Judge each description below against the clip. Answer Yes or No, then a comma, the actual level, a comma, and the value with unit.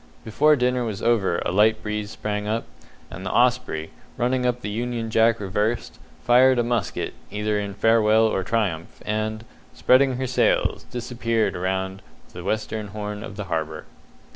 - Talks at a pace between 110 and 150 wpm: No, average, 160 wpm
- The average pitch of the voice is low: Yes, low, 110 Hz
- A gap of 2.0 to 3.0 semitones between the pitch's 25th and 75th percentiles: Yes, average, 2.7 semitones